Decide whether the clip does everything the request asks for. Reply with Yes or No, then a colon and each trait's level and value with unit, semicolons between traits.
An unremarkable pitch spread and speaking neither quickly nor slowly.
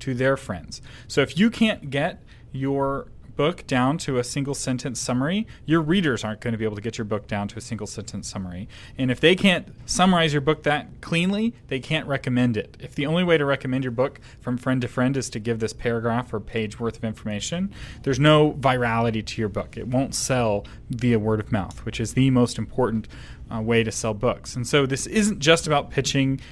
No: average, 4.0 semitones; fast, 220 wpm